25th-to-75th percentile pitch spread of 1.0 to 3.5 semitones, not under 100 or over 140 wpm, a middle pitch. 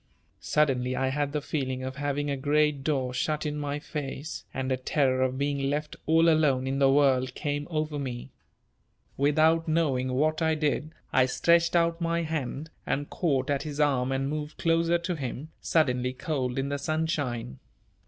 No: average, 2.8 semitones; average, 175 wpm; medium, 145 Hz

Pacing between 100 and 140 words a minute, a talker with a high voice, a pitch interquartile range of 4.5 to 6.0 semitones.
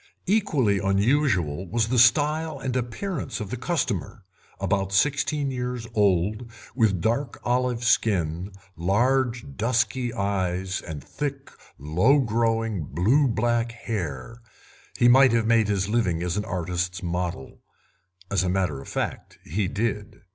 No: slow, 135 wpm; low, 110 Hz; average, 5.2 semitones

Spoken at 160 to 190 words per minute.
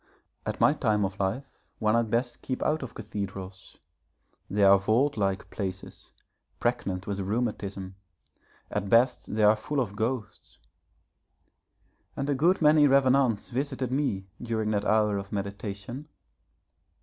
No: slow, 135 wpm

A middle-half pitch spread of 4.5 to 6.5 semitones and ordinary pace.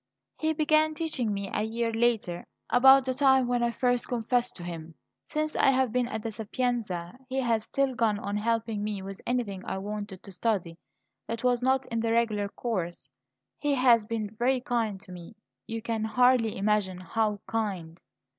No: average, 3.4 semitones; average, 185 wpm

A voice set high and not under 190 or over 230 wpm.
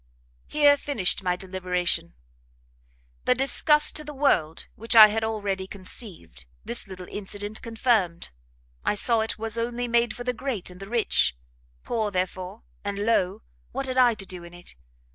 No: high, 215 Hz; average, 160 wpm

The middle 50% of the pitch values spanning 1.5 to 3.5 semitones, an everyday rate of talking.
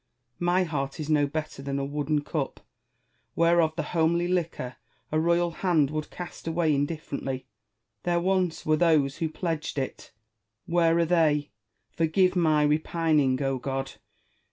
Yes: average, 2.9 semitones; average, 145 wpm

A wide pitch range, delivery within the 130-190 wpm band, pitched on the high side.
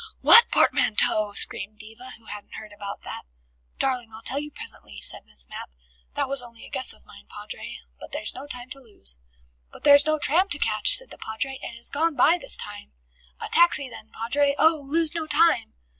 No: wide, 5.7 semitones; fast, 205 wpm; very high, 255 Hz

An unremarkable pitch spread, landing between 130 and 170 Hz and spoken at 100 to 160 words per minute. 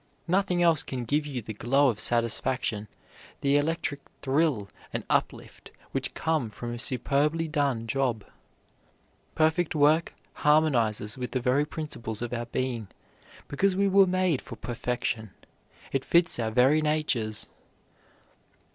Yes: average, 4.8 semitones; low, 135 Hz; slow, 135 wpm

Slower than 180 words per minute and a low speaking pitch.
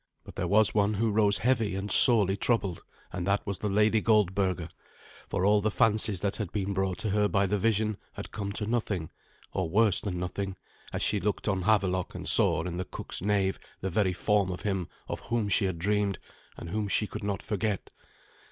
No: fast, 205 wpm; low, 100 Hz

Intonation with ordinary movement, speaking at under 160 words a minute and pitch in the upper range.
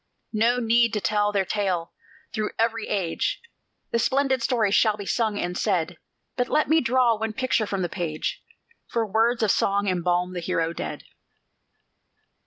No: average, 4.2 semitones; average, 165 wpm; high, 210 Hz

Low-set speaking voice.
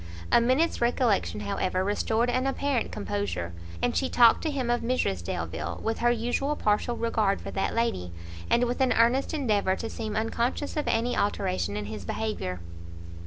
No: high, 225 Hz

